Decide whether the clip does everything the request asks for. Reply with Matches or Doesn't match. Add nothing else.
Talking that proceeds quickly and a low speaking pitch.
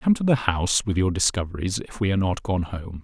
Matches